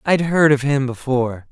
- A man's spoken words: Yes, male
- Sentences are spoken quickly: Yes, fast, 240 wpm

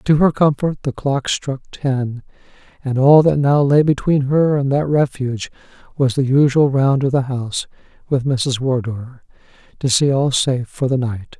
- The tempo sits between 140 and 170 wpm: No, average, 180 wpm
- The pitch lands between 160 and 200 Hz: No, low, 135 Hz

